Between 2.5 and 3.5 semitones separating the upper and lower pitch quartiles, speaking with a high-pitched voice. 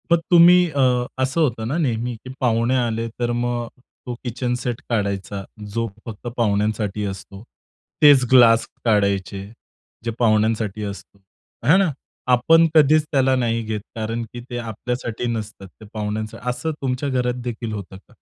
No: average, 2.9 semitones; low, 115 Hz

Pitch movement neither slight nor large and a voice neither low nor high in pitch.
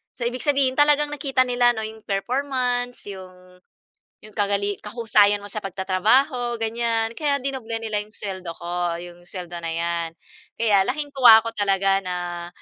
No: average, 4.7 semitones; high, 215 Hz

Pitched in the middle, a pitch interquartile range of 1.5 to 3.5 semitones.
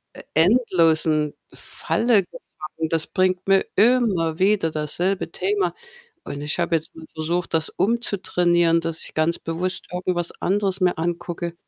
Yes: medium, 175 Hz; average, 2.9 semitones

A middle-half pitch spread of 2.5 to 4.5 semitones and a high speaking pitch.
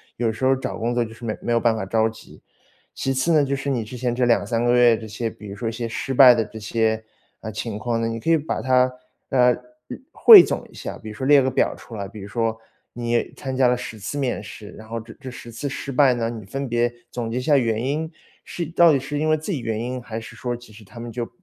No: average, 2.8 semitones; low, 120 Hz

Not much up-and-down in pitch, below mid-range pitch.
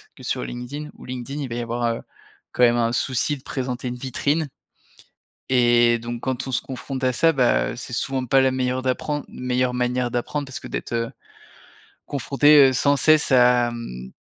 Yes: narrow, 2.0 semitones; low, 125 Hz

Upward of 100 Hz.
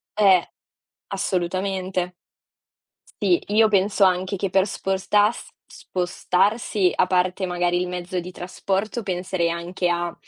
Yes: medium, 185 Hz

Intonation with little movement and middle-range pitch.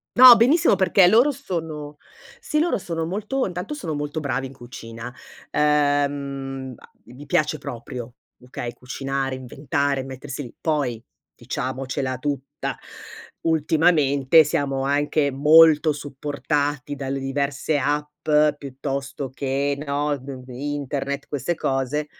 Yes: narrow, 2.2 semitones; medium, 145 Hz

